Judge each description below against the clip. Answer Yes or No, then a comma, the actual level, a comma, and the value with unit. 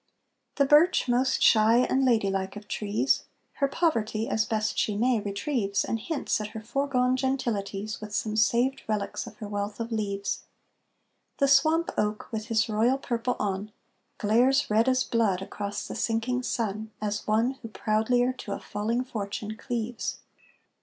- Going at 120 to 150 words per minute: No, average, 160 wpm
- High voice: Yes, high, 225 Hz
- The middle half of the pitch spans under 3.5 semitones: Yes, average, 3.1 semitones